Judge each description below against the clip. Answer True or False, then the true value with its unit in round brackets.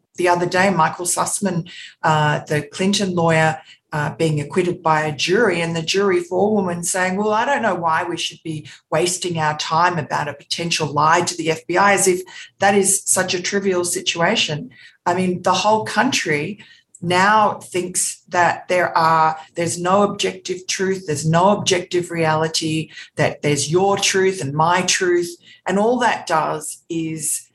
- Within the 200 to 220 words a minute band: False (165 wpm)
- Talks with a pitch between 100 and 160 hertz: False (175 Hz)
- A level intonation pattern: False (3.0 semitones)